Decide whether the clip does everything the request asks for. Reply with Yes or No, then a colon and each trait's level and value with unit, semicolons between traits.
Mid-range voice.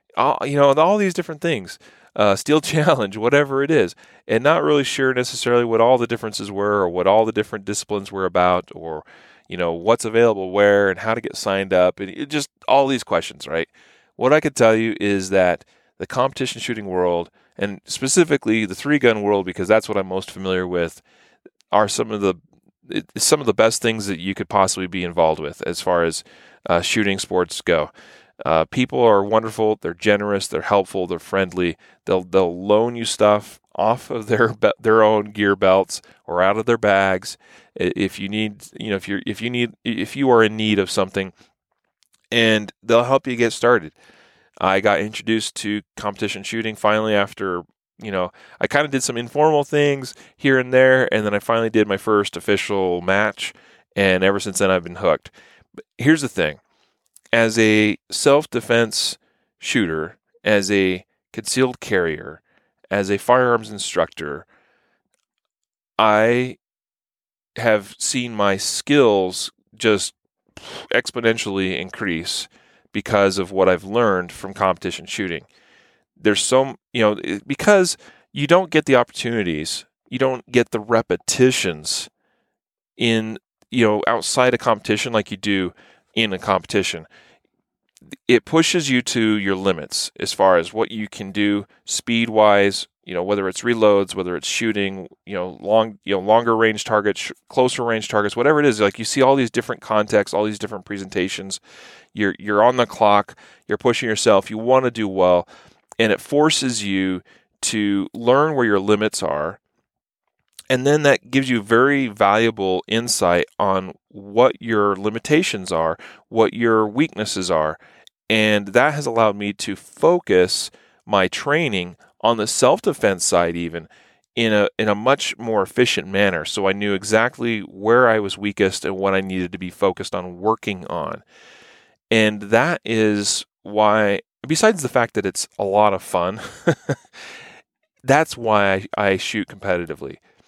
No: low, 105 Hz